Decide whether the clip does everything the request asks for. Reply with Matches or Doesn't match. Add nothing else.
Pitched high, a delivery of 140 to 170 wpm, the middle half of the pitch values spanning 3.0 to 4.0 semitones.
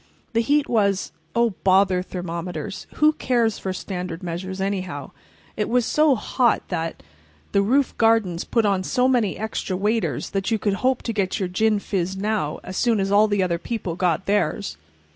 Matches